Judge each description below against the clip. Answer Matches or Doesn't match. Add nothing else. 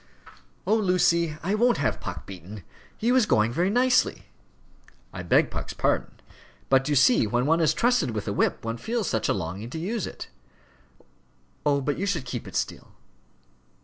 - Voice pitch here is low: Doesn't match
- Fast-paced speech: Doesn't match